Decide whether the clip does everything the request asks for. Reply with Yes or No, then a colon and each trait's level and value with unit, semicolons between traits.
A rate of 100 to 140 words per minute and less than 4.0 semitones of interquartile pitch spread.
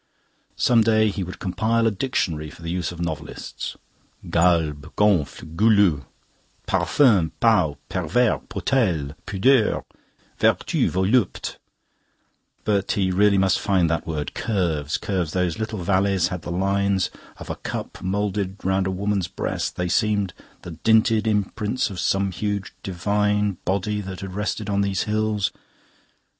Yes: slow, 135 wpm; average, 3.0 semitones